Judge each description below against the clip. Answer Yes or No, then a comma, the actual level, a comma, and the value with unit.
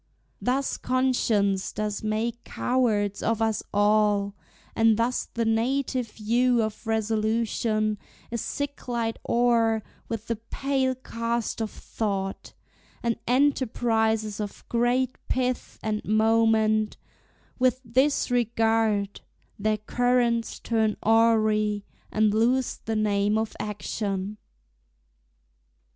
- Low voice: No, high, 225 Hz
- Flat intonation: Yes, narrow, 2.0 semitones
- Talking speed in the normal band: No, slow, 100 wpm